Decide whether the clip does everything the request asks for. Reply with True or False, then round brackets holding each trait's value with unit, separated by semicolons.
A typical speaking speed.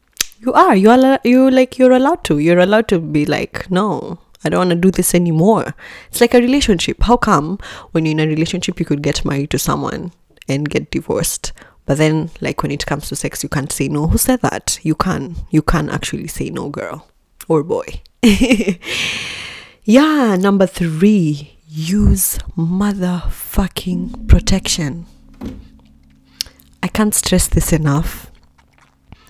True (160 wpm)